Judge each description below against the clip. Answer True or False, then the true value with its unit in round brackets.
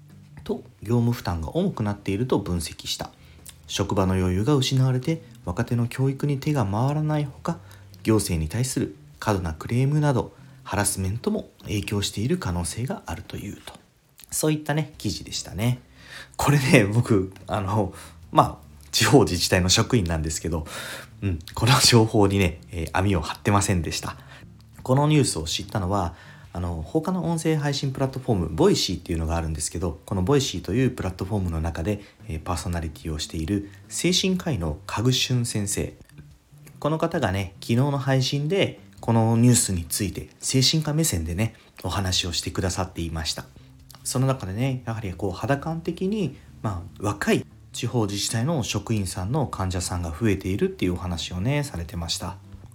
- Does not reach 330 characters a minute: False (360 characters per minute)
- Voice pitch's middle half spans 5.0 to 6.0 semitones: False (6.5 semitones)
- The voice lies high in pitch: False (105 Hz)